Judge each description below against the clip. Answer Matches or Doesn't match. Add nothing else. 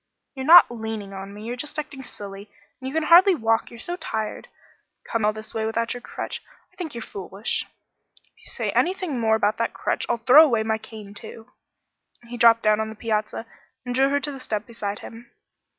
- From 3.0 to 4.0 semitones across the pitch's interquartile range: Matches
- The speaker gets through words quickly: Matches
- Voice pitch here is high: Matches